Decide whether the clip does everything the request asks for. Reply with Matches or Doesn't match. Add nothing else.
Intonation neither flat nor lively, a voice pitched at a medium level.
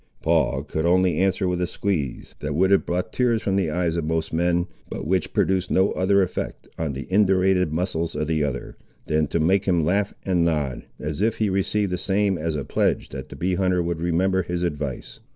Doesn't match